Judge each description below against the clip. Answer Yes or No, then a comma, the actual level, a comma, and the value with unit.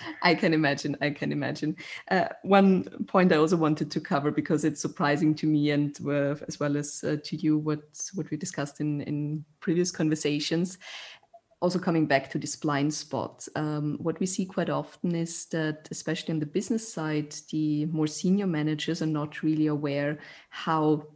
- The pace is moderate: Yes, average, 180 wpm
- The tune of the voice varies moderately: No, narrow, 1.9 semitones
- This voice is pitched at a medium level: Yes, medium, 155 Hz